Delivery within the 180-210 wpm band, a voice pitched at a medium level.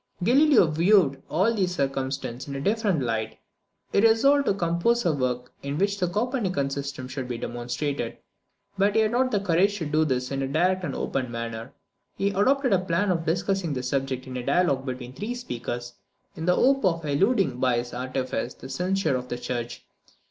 Yes: average, 190 wpm; medium, 155 Hz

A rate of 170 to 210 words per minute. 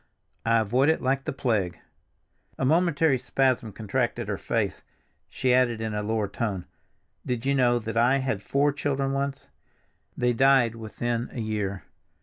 No: average, 155 wpm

